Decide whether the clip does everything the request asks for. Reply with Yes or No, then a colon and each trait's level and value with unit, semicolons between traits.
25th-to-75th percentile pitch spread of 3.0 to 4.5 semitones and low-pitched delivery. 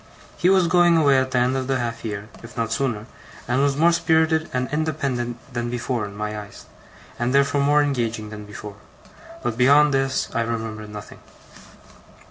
Yes: average, 4.2 semitones; low, 125 Hz